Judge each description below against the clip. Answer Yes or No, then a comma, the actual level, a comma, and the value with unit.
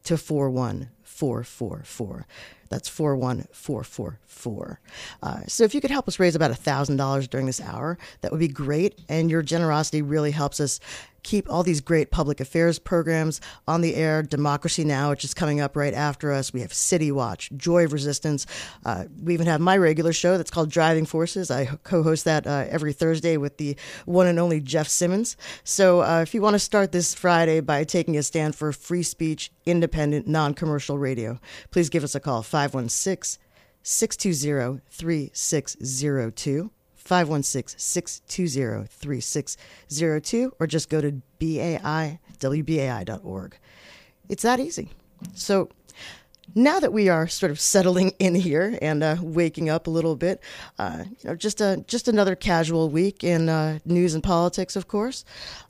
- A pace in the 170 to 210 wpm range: No, average, 160 wpm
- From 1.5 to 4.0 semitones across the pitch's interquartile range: Yes, average, 3.4 semitones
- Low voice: No, medium, 160 Hz